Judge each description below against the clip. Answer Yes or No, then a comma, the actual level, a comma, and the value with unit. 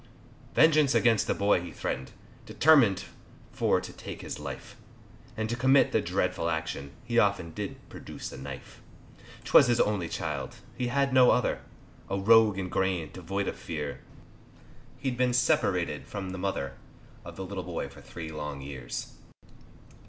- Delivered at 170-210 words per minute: No, average, 160 wpm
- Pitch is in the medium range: No, very low, 95 Hz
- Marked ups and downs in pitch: Yes, wide, 6.7 semitones